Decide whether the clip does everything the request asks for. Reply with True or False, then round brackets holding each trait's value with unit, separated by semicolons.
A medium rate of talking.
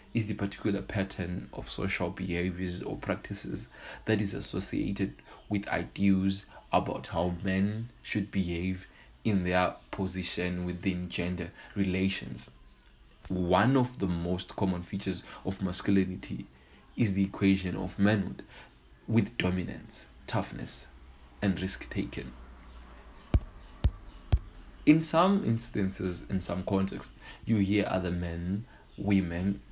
False (110 wpm)